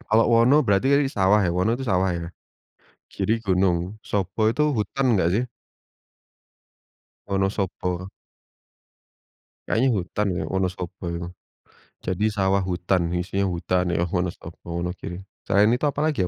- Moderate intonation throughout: Yes, average, 3.4 semitones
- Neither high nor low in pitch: No, very low, 95 Hz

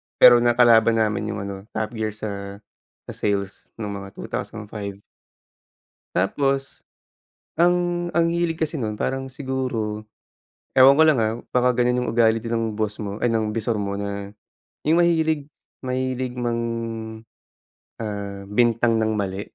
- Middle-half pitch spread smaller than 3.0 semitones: No, average, 4.0 semitones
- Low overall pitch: Yes, low, 115 Hz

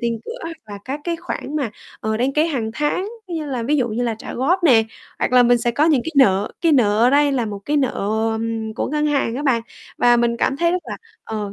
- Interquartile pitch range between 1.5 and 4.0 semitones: No, average, 4.7 semitones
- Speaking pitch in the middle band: No, very high, 255 Hz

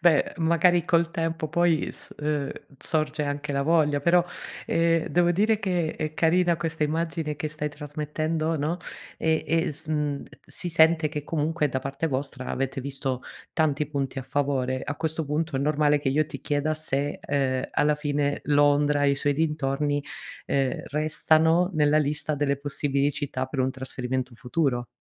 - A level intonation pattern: Yes, narrow, 2.3 semitones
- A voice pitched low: No, medium, 150 Hz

